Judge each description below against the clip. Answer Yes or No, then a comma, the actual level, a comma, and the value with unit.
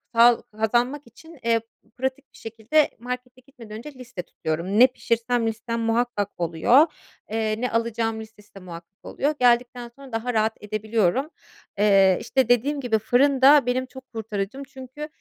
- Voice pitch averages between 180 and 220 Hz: No, high, 235 Hz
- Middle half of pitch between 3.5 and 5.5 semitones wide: No, average, 3.0 semitones